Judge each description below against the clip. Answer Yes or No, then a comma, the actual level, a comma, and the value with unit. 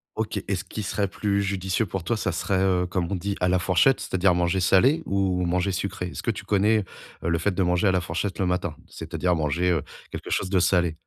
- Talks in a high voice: No, very low, 95 Hz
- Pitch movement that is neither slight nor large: No, narrow, 1.9 semitones